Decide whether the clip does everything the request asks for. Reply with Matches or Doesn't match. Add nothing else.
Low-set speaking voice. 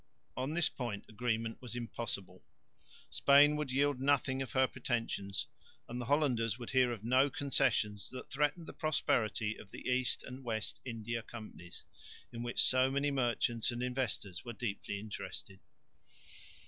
Matches